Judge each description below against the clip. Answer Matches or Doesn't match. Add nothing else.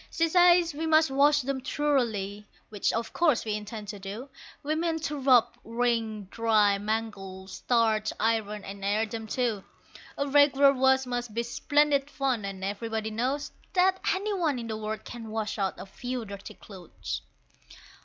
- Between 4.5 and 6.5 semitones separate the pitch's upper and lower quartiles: Matches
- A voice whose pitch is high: Matches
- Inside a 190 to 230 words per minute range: Doesn't match